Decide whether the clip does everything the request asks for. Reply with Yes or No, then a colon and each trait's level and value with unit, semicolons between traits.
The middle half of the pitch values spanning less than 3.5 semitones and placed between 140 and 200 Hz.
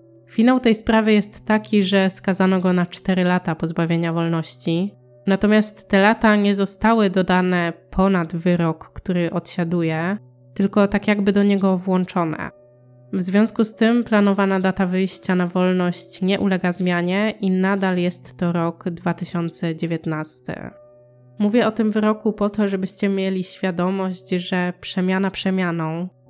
Yes: average, 2.7 semitones; medium, 185 Hz